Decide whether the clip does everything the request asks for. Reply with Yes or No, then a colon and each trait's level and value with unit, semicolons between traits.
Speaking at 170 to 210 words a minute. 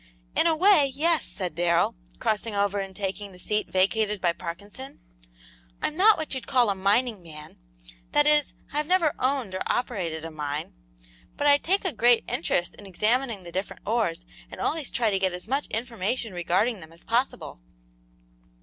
Yes: average, 175 wpm